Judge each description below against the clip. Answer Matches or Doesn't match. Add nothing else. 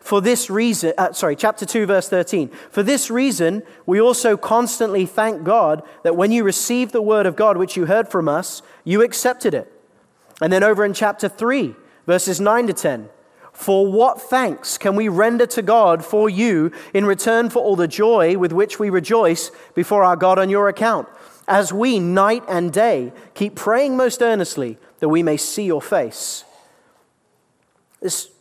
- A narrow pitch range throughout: Doesn't match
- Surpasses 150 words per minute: Matches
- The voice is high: Matches